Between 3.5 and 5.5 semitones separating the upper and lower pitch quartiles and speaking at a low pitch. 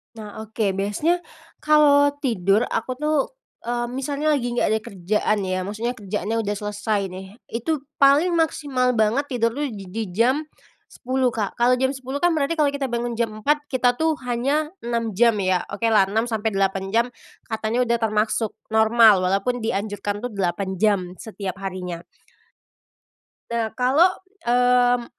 No: average, 4.1 semitones; high, 230 Hz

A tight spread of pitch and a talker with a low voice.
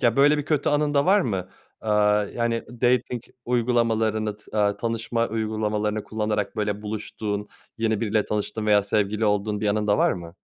Yes: narrow, 2.0 semitones; low, 110 Hz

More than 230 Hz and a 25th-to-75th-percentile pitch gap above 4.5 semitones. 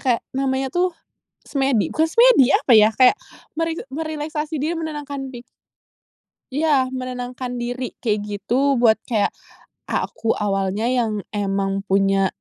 Yes: very high, 255 Hz; average, 5.2 semitones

